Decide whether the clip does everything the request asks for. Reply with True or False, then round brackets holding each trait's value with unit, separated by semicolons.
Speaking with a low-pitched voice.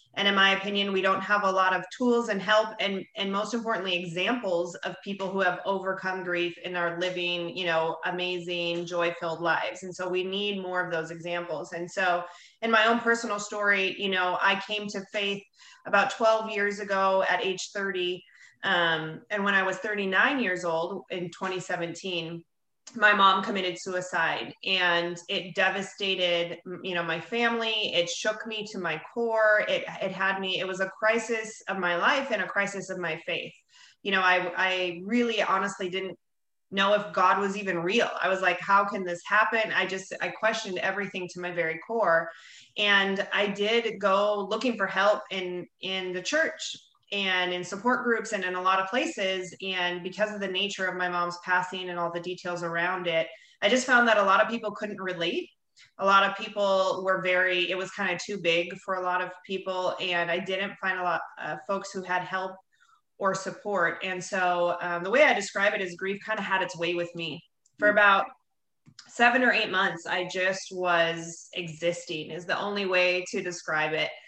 False (190 Hz)